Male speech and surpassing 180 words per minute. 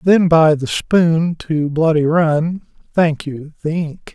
No: male; average, 145 wpm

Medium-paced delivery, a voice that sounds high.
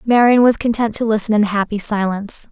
Yes: average, 190 wpm; high, 220 Hz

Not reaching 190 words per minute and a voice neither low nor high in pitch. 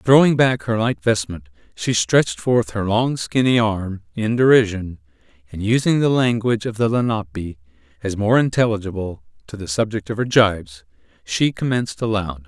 No: average, 160 wpm; low, 105 Hz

